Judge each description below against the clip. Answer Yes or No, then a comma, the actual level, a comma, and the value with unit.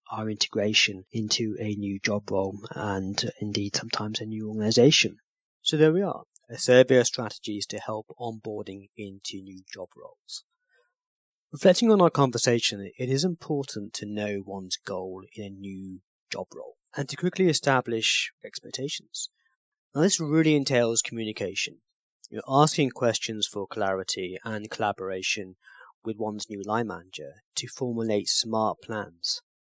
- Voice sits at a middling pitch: No, low, 110 Hz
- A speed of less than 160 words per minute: Yes, average, 140 wpm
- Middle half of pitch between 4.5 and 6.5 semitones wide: Yes, average, 5.1 semitones